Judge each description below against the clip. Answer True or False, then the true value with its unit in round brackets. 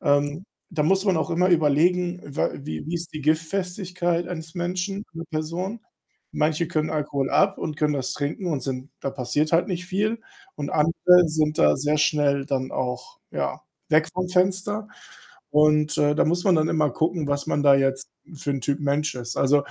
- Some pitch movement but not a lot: True (3.7 semitones)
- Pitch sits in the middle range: True (155 Hz)